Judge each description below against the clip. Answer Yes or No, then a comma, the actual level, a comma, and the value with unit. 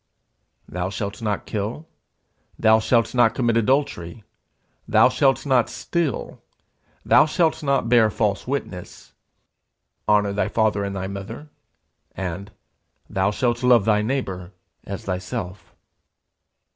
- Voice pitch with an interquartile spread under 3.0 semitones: No, average, 4.1 semitones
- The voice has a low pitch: Yes, low, 110 Hz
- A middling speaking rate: No, slow, 120 wpm